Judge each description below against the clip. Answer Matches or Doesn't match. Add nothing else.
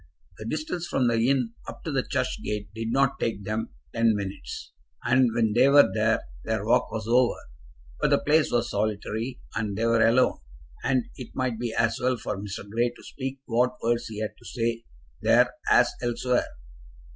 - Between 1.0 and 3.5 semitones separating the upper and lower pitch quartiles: Matches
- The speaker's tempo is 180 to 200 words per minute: Matches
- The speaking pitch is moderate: Doesn't match